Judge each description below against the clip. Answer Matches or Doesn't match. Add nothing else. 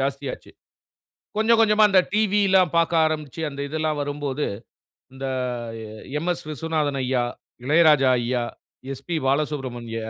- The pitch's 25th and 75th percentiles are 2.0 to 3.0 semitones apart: Doesn't match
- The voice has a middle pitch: Matches